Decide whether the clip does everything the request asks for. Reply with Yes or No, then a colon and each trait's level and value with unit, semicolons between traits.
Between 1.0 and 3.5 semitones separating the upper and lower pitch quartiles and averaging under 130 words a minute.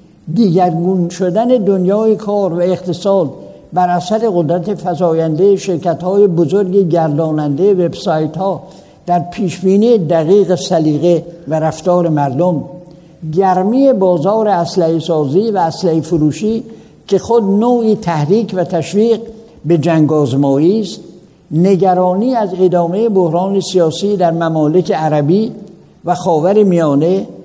Yes: average, 2.9 semitones; average, 110 wpm